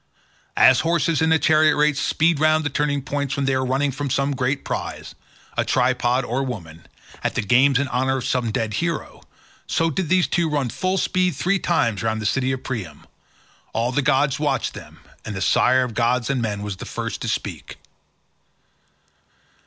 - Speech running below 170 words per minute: No, average, 185 wpm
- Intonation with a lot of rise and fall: No, average, 3.7 semitones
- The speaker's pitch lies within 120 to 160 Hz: Yes, low, 135 Hz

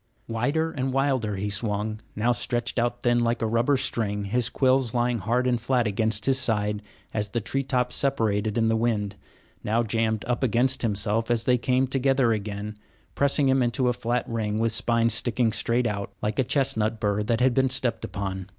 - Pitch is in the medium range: No, low, 115 Hz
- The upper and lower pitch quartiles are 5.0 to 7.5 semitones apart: No, average, 2.8 semitones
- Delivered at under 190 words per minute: No, average, 195 wpm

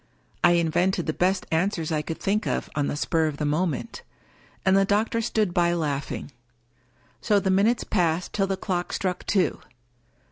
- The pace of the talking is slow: No, average, 175 wpm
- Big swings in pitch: No, average, 3.5 semitones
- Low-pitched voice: No, medium, 180 Hz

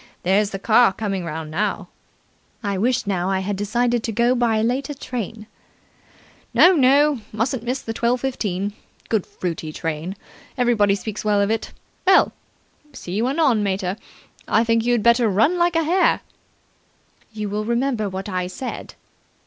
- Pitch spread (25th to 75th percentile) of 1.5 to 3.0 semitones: No, average, 3.9 semitones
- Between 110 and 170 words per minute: Yes, average, 160 wpm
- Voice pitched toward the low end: No, high, 220 Hz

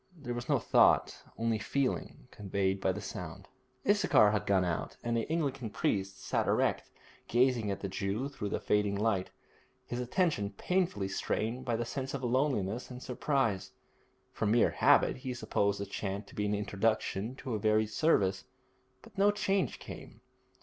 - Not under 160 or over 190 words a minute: Yes, average, 170 wpm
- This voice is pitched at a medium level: No, low, 110 Hz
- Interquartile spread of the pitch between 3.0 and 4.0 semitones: No, average, 4.6 semitones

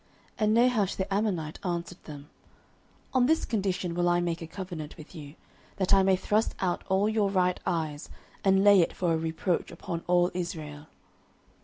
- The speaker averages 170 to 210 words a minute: Yes, average, 180 wpm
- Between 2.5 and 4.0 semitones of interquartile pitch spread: Yes, average, 3.1 semitones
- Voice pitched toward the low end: No, medium, 180 Hz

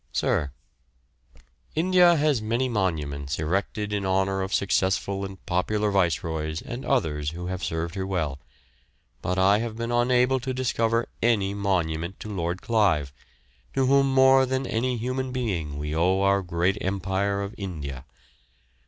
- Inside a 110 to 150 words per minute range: Yes, average, 145 wpm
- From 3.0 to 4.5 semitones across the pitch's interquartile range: No, wide, 5.6 semitones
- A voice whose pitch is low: Yes, low, 100 Hz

